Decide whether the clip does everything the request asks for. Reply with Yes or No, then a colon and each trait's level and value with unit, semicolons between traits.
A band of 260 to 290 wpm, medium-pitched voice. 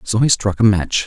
No: fast, 280 wpm; low, 105 Hz